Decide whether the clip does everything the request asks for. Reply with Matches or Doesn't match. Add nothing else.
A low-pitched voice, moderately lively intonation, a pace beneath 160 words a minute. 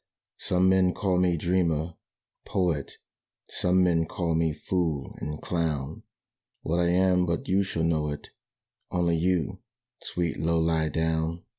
Doesn't match